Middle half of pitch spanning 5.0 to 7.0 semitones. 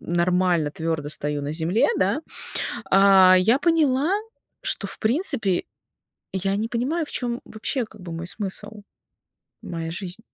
Yes: wide, 5.6 semitones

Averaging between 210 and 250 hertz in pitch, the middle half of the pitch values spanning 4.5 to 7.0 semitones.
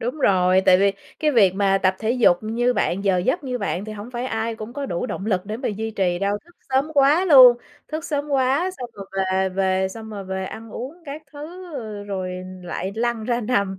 Yes: high, 220 Hz; average, 5.1 semitones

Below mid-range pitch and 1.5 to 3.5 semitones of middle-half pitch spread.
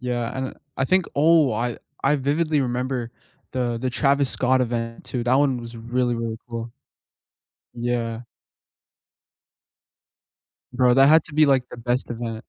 Yes: low, 125 Hz; narrow, 2.5 semitones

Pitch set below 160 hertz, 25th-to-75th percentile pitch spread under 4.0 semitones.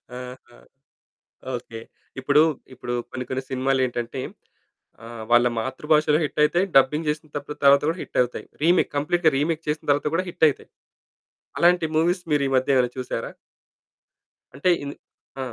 Yes: medium, 140 Hz; average, 3.3 semitones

